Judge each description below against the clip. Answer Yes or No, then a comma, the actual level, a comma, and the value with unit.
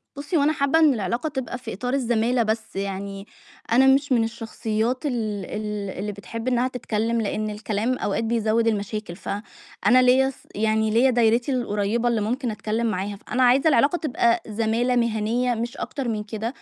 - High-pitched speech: Yes, high, 230 Hz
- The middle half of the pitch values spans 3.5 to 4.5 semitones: No, average, 2.8 semitones